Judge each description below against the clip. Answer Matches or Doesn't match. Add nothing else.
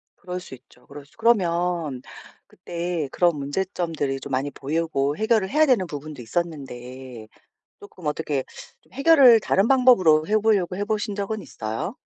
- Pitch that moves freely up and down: Matches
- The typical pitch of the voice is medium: Matches